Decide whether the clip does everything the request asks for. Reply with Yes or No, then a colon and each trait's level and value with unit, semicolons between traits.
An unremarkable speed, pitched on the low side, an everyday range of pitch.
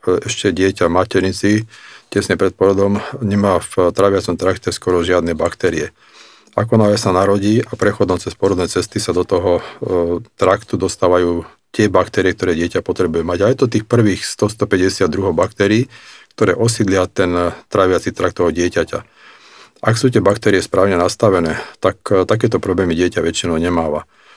Yes: average, 145 wpm; low, 100 Hz; average, 3.4 semitones